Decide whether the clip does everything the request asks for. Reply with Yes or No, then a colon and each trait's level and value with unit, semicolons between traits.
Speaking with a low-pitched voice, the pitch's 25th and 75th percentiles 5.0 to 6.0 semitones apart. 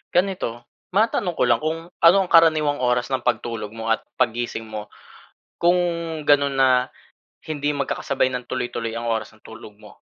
Yes: low, 130 Hz; average, 5.3 semitones